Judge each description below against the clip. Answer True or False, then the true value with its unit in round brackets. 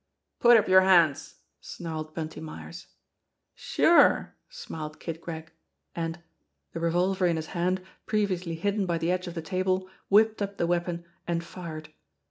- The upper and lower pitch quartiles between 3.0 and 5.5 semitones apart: False (2.4 semitones)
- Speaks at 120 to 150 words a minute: False (160 wpm)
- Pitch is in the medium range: True (175 Hz)